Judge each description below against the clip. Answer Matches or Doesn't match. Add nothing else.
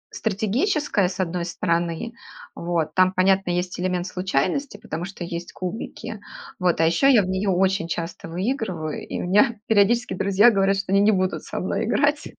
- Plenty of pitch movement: Doesn't match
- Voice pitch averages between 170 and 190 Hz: Matches